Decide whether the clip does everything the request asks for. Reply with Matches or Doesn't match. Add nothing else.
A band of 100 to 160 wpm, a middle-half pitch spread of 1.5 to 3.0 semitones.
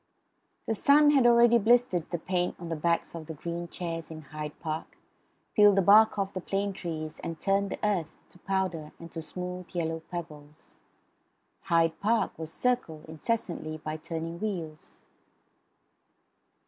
Doesn't match